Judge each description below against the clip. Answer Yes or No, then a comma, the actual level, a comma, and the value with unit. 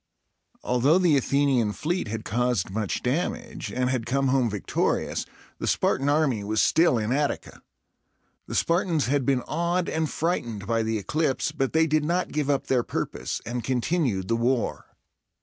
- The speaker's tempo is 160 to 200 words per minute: Yes, average, 165 wpm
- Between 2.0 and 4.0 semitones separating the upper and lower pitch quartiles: No, average, 5.1 semitones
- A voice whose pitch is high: No, low, 130 Hz